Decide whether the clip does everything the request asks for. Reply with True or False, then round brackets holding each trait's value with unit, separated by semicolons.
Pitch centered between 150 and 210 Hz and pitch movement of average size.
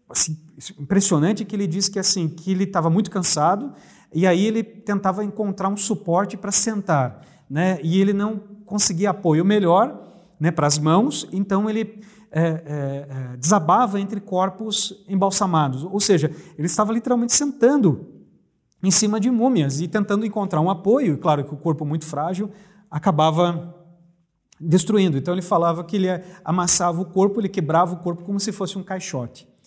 True (190 Hz; 3.5 semitones)